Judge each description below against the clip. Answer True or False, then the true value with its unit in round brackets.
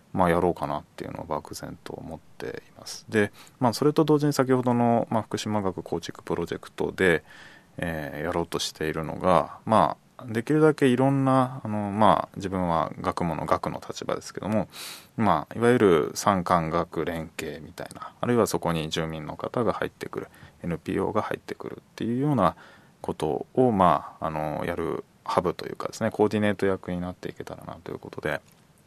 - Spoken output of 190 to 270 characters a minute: False (380 characters per minute)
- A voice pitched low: True (105 Hz)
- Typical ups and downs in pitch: False (6.9 semitones)